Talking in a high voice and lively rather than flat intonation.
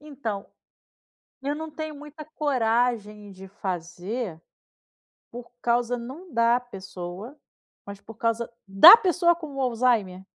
Yes: high, 235 Hz; wide, 6.1 semitones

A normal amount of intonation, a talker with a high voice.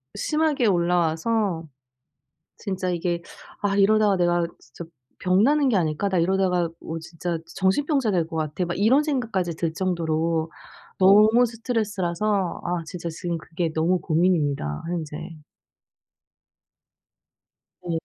No: average, 3.8 semitones; medium, 180 Hz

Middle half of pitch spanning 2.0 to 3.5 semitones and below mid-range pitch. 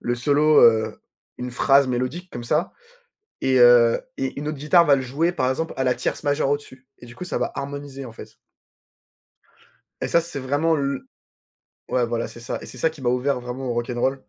Yes: average, 2.9 semitones; low, 130 Hz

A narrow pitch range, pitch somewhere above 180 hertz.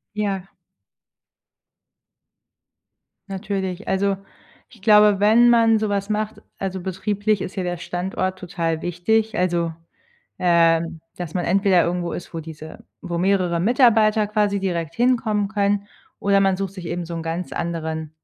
No: average, 3.3 semitones; high, 190 Hz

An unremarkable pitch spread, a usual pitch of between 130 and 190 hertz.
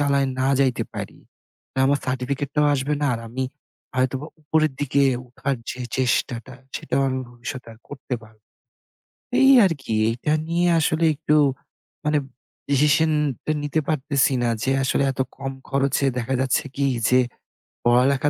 No: narrow, 2.3 semitones; medium, 140 Hz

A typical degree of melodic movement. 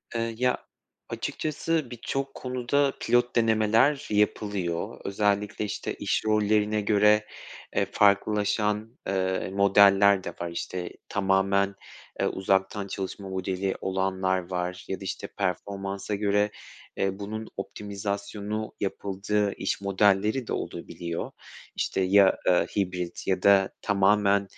No: narrow, 1.7 semitones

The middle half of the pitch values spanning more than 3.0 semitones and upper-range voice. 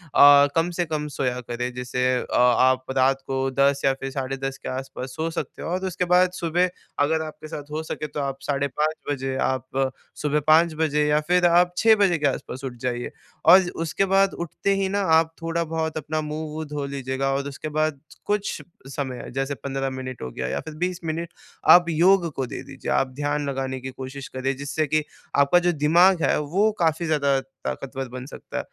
No: average, 3.4 semitones; medium, 145 Hz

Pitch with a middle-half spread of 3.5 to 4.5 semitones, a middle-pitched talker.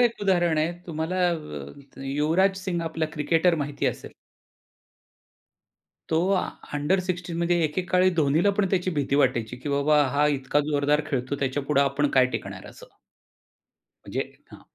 Yes: average, 3.8 semitones; medium, 155 Hz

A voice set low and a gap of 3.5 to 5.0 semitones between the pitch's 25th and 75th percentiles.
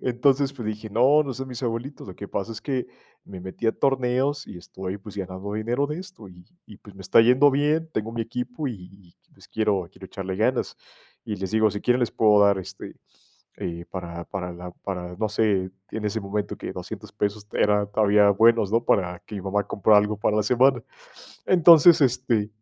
Yes: low, 105 Hz; average, 4.2 semitones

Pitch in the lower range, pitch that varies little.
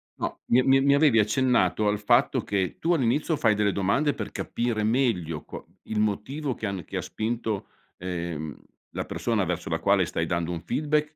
No: low, 110 Hz; wide, 5.8 semitones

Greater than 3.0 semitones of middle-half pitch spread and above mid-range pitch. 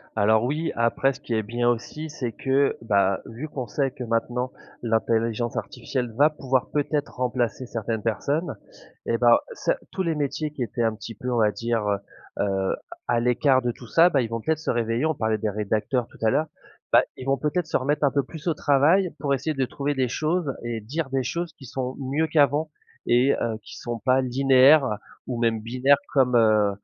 No: average, 3.7 semitones; low, 125 Hz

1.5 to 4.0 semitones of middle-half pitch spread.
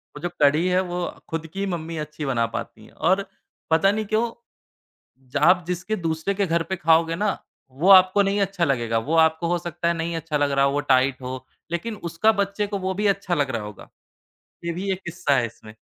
No: average, 4.6 semitones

